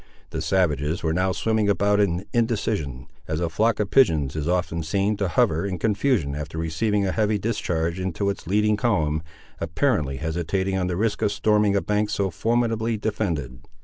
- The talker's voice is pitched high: No, very low, 95 Hz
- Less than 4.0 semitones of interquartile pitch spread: No, average, 4.7 semitones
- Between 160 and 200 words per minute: Yes, average, 180 wpm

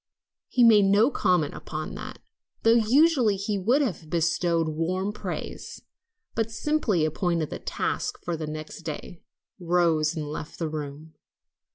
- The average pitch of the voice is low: No, medium, 175 Hz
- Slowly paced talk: No, average, 145 wpm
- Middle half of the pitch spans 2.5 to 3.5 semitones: No, wide, 5.5 semitones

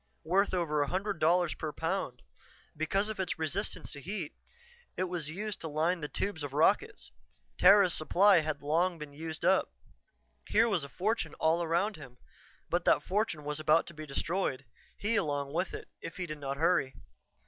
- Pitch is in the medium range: Yes, medium, 165 Hz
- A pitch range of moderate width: Yes, average, 3.9 semitones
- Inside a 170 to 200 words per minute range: Yes, average, 180 wpm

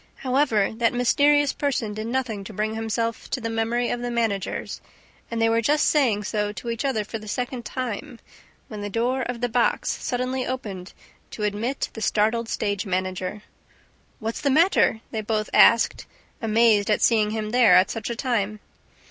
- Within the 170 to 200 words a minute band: Yes, average, 180 wpm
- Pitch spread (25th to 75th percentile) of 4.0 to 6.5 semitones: No, narrow, 2.6 semitones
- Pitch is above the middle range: Yes, high, 225 Hz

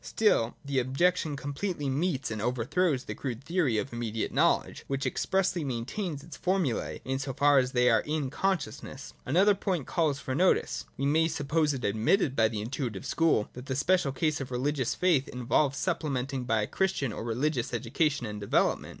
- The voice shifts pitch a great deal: No, average, 4.6 semitones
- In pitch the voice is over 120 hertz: Yes, low, 135 Hz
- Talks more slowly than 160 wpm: No, average, 185 wpm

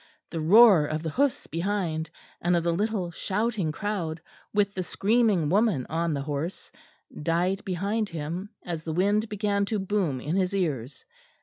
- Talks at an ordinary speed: Yes, average, 165 wpm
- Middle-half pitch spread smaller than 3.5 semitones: No, average, 4.2 semitones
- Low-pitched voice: No, medium, 180 Hz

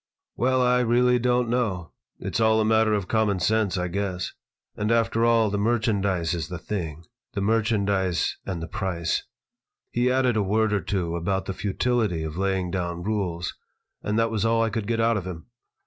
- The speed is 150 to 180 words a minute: No, average, 190 wpm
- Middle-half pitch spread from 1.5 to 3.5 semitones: No, average, 3.9 semitones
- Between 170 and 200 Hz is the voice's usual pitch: No, low, 105 Hz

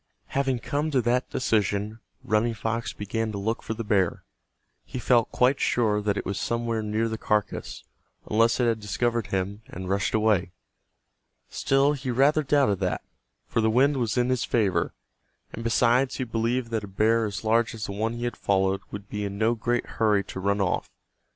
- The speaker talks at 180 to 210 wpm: Yes, average, 190 wpm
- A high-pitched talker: No, low, 115 Hz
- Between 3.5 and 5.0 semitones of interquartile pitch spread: No, average, 2.8 semitones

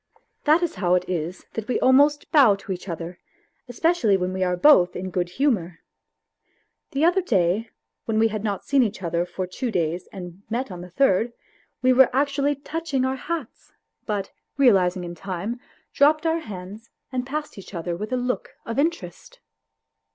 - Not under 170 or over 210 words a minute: Yes, average, 180 wpm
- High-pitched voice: Yes, high, 220 Hz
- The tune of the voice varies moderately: No, wide, 7.2 semitones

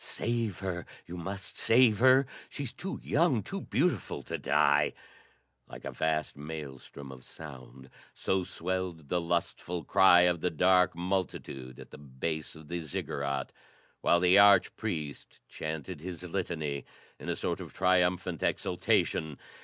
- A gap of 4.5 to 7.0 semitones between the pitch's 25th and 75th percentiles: No, average, 3.8 semitones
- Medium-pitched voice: No, very low, 85 Hz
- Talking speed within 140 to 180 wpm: Yes, average, 145 wpm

